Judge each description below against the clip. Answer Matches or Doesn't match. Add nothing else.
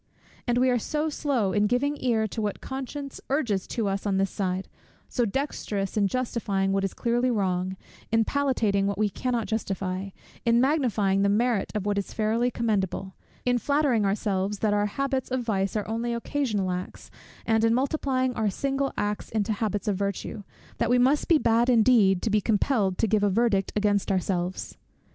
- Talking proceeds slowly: Doesn't match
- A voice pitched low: Doesn't match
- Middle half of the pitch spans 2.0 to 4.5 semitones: Matches